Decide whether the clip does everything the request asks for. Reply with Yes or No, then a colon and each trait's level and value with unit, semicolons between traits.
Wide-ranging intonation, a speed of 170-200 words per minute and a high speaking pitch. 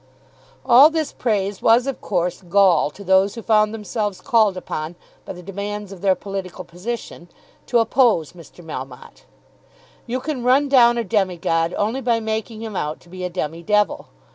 No: average, 4.6 semitones; average, 175 wpm; high, 205 Hz